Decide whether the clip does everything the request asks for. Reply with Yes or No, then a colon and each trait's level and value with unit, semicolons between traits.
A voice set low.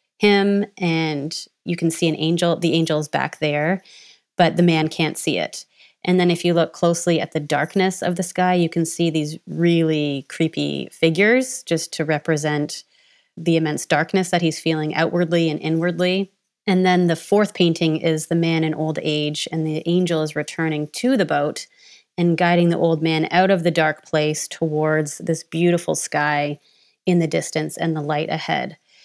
No: medium, 165 Hz